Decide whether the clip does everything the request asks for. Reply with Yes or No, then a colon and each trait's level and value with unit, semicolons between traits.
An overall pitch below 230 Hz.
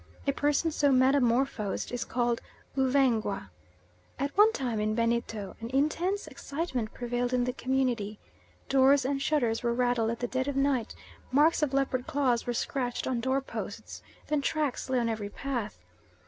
No: very high, 255 Hz